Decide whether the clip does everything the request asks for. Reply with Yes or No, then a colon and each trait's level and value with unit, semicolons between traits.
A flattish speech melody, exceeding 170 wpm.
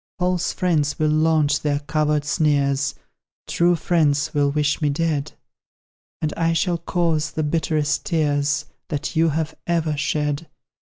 No: narrow, 2.0 semitones; slow, 135 wpm